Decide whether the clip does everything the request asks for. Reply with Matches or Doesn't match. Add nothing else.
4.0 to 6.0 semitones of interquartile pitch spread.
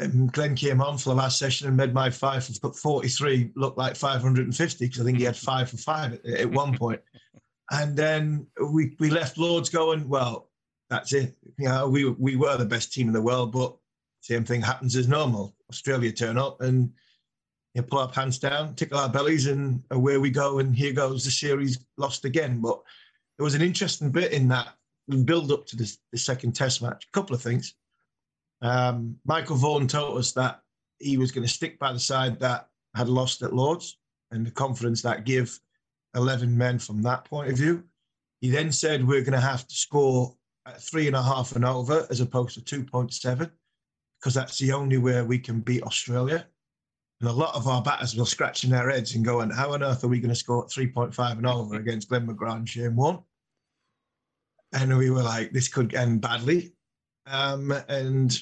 Doesn't match